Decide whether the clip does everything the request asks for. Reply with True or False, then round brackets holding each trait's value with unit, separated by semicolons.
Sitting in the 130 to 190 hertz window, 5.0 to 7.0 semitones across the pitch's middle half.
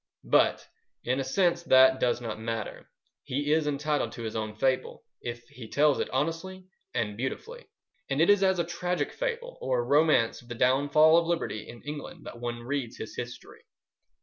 True (135 Hz; 5.5 semitones)